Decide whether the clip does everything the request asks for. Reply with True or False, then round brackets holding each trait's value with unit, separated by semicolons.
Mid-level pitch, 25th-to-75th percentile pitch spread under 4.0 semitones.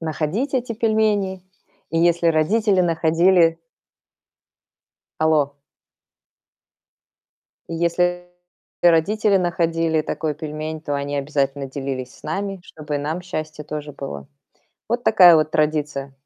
True (160 Hz; 3.3 semitones)